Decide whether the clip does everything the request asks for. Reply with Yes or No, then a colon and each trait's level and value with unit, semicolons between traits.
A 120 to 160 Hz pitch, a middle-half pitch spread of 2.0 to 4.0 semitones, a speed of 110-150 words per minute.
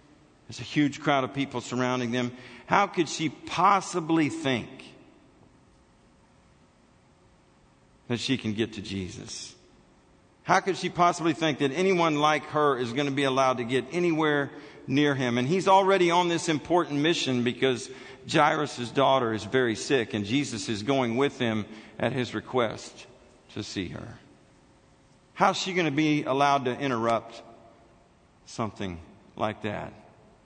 No: low, 135 Hz; average, 5.0 semitones; average, 145 wpm